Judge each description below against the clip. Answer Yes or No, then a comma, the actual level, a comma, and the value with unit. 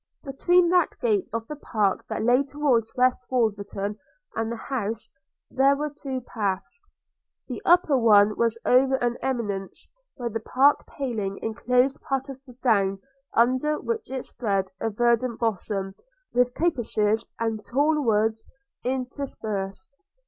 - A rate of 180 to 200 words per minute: No, average, 140 wpm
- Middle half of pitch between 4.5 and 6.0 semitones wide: No, average, 3.9 semitones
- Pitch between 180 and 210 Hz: No, high, 240 Hz